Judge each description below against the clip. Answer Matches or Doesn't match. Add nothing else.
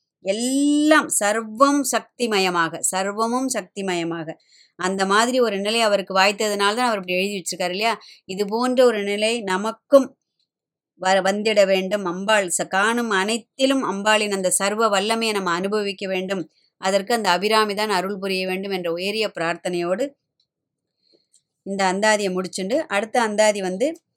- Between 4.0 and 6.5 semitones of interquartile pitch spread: Doesn't match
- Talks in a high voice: Matches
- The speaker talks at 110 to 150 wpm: Matches